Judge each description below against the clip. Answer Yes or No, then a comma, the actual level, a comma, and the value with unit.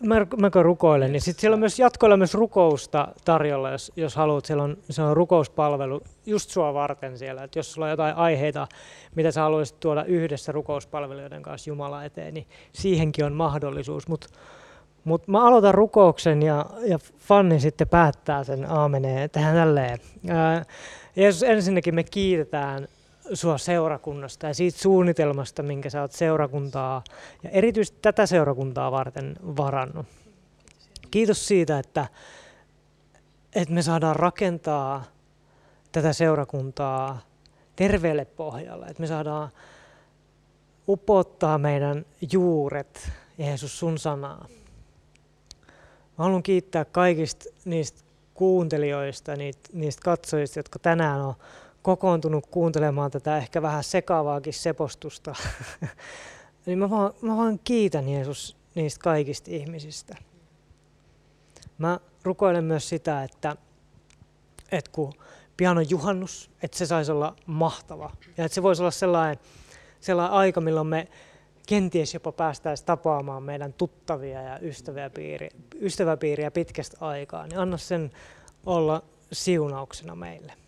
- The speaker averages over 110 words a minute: Yes, average, 125 wpm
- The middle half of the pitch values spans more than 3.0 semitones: Yes, average, 3.4 semitones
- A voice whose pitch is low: No, medium, 155 Hz